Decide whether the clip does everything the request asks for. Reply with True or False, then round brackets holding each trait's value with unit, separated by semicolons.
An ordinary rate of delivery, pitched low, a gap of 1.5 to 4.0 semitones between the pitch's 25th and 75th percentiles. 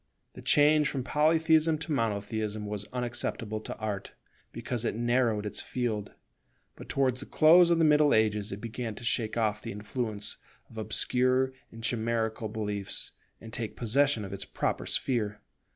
True (160 wpm; 115 Hz; 3.7 semitones)